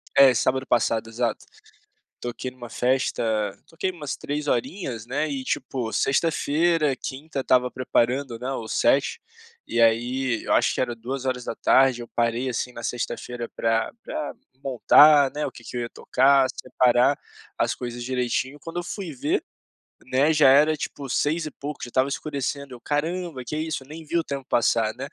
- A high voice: No, low, 130 Hz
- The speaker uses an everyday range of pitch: Yes, average, 3.3 semitones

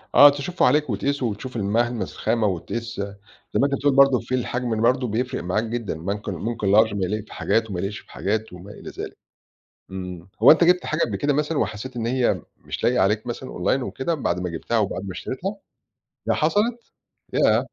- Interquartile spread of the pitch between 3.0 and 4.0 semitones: No, average, 4.8 semitones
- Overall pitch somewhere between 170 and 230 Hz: No, low, 115 Hz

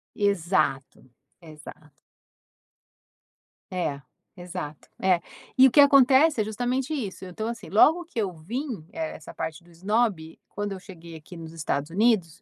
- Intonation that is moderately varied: No, wide, 6.4 semitones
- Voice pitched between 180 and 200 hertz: Yes, medium, 185 Hz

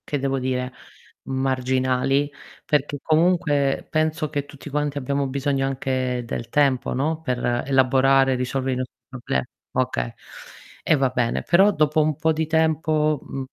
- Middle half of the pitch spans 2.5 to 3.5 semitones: Yes, average, 2.8 semitones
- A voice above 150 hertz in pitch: No, low, 135 Hz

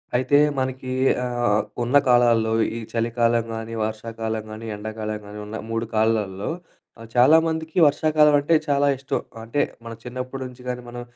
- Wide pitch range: No, average, 2.9 semitones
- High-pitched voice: No, low, 120 Hz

